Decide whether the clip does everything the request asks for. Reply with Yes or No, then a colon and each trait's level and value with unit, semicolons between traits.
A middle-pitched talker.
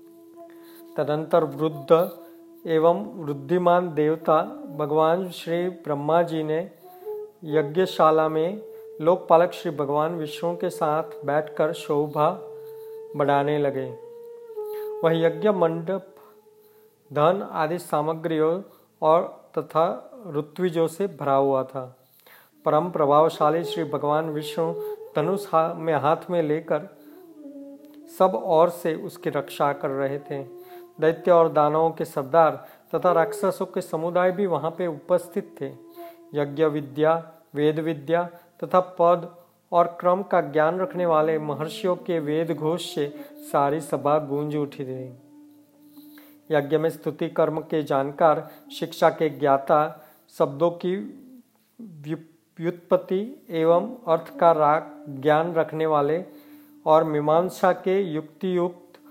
Yes: medium, 165 Hz